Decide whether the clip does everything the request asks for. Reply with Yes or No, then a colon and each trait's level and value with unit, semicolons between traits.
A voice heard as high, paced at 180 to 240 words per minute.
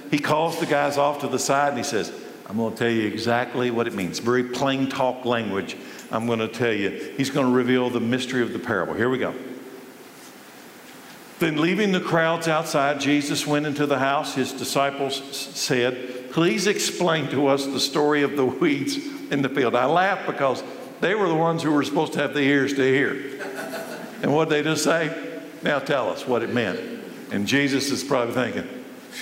No: medium, 140 Hz; fast, 205 wpm